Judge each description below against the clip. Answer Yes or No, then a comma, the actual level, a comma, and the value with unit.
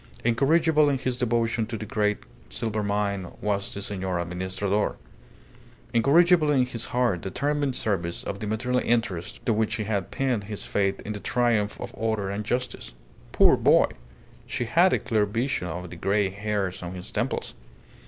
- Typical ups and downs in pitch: Yes, average, 3.8 semitones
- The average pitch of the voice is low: Yes, low, 105 Hz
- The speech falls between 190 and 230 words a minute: No, average, 170 wpm